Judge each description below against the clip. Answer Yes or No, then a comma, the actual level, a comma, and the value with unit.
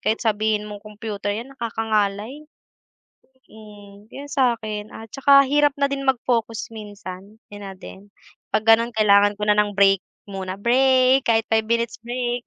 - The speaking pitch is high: Yes, high, 220 Hz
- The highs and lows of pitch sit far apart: No, average, 3.0 semitones